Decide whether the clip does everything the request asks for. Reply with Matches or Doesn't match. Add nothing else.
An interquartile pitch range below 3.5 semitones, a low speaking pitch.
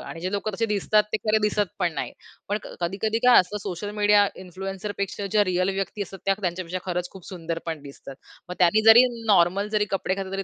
Doesn't match